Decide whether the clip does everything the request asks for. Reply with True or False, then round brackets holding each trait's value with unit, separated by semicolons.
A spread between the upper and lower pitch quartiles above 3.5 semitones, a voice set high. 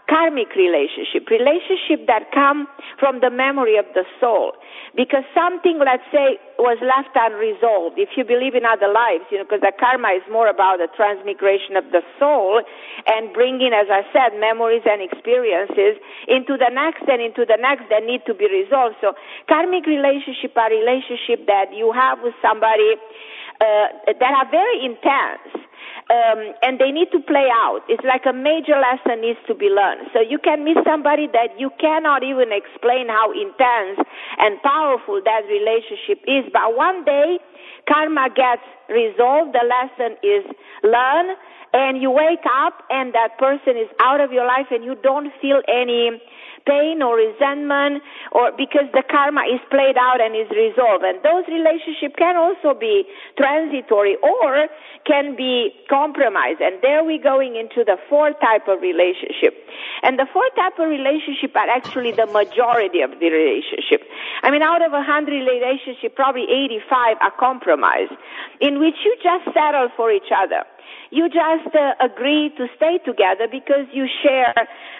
True (4.9 semitones; 270 Hz)